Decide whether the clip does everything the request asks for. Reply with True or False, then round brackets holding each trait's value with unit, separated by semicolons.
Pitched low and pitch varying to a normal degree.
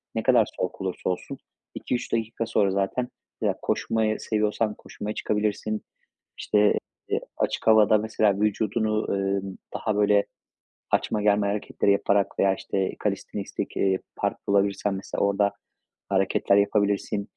False (105 Hz; 1.5 semitones)